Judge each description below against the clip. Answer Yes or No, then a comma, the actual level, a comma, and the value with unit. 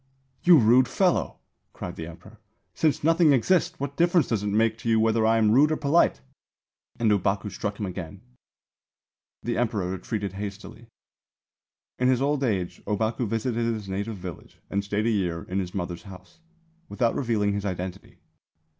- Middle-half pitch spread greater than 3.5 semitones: Yes, average, 4.2 semitones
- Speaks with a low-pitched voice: Yes, low, 110 Hz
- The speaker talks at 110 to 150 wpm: No, average, 165 wpm